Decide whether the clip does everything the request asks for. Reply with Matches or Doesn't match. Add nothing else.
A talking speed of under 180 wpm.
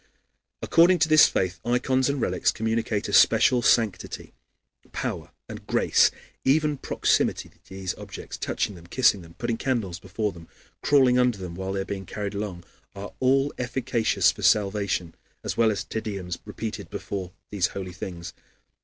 Matches